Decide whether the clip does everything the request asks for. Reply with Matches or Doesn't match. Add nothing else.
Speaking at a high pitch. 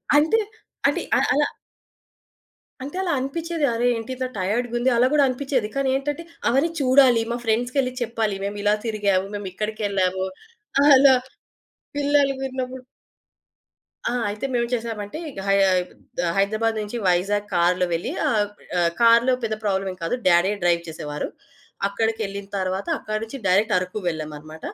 Matches